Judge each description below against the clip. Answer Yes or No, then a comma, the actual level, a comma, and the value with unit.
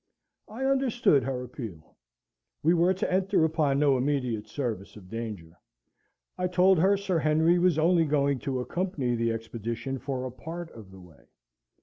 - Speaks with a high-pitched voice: No, medium, 140 Hz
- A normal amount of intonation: No, wide, 7.0 semitones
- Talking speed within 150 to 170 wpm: Yes, average, 160 wpm